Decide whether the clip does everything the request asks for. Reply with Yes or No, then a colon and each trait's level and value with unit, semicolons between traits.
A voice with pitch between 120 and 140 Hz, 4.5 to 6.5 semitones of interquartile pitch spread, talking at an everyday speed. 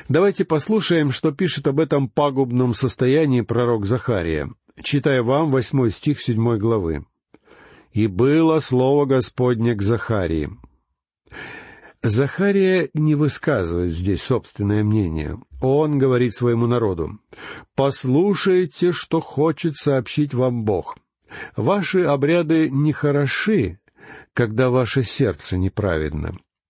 No: low, 130 Hz; average, 5.1 semitones; slow, 100 wpm